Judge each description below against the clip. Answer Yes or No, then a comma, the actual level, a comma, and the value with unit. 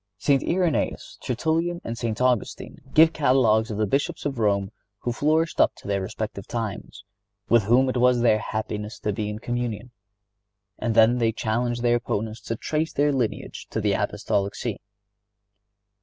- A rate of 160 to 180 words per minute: Yes, average, 165 wpm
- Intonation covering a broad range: No, average, 3.3 semitones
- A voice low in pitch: Yes, low, 120 Hz